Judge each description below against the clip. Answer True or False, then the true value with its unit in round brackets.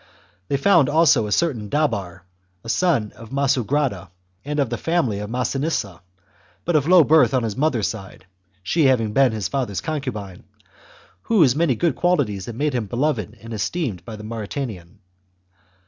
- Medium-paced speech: True (165 wpm)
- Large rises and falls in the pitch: True (6.0 semitones)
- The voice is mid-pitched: False (125 Hz)